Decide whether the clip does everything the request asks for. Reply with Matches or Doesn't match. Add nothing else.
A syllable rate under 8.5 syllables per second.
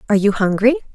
Matches